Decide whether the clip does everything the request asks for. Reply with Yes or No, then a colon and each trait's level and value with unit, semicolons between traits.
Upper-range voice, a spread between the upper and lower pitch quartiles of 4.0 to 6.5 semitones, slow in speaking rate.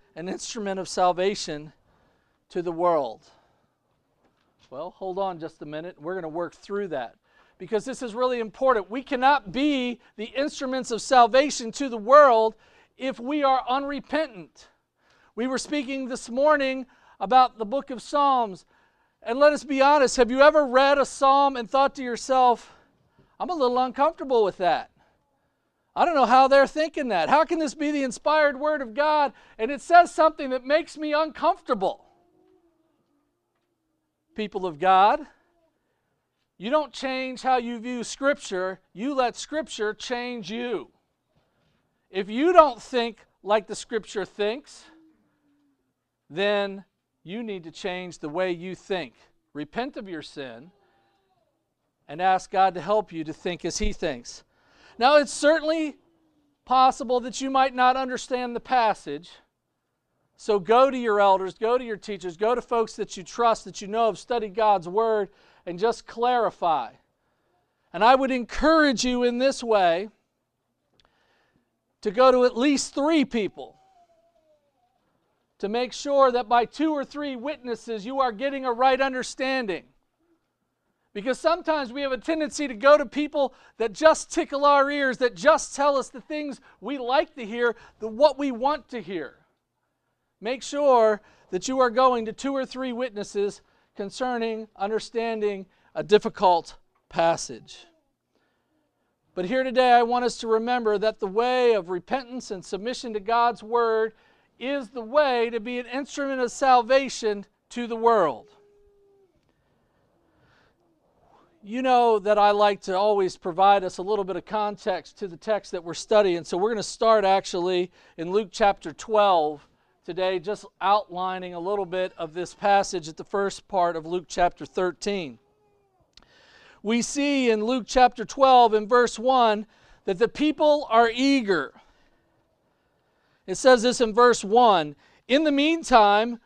No: high, 240 Hz; average, 5.2 semitones; average, 155 wpm